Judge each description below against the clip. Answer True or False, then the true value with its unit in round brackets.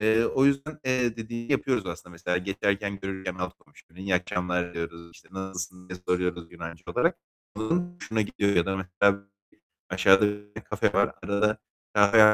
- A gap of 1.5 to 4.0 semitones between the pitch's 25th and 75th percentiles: True (3.4 semitones)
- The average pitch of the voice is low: True (95 Hz)